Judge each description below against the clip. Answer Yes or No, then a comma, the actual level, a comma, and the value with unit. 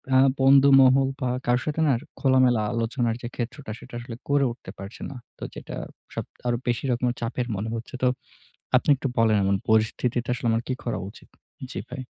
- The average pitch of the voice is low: Yes, low, 125 Hz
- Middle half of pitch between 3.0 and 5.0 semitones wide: No, narrow, 2.5 semitones